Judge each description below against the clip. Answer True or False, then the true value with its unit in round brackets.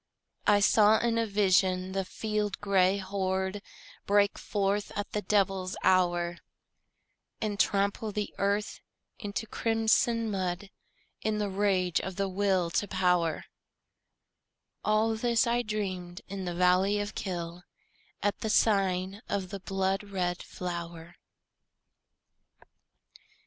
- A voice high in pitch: True (195 Hz)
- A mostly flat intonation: True (2.1 semitones)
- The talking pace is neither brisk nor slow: False (120 wpm)